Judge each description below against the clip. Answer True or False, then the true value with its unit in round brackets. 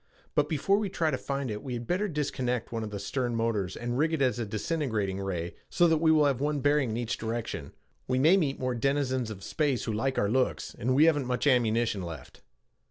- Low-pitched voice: True (130 Hz)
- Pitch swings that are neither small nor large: True (4.7 semitones)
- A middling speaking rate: False (235 wpm)